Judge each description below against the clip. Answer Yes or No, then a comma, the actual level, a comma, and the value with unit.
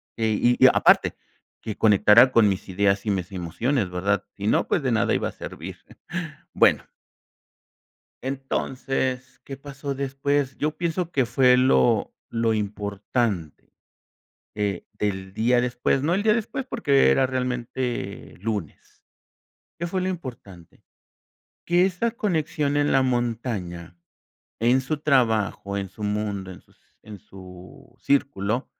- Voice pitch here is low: Yes, low, 120 Hz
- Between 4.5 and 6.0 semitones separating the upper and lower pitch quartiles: Yes, average, 5.3 semitones